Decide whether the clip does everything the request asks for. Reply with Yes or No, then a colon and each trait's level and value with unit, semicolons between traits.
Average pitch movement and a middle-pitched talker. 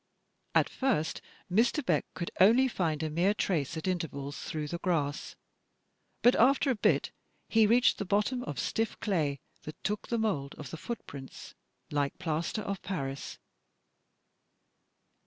No: wide, 6.6 semitones; medium, 180 Hz